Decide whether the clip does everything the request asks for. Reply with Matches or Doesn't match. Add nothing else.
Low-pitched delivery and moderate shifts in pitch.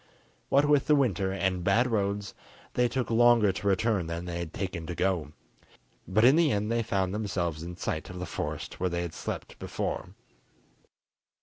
Matches